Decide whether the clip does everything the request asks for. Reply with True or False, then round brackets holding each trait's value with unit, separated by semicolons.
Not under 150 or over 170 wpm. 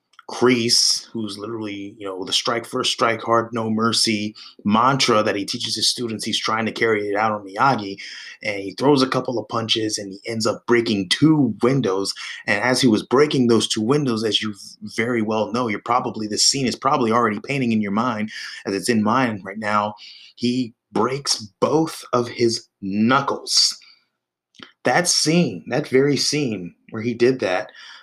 False (180 wpm)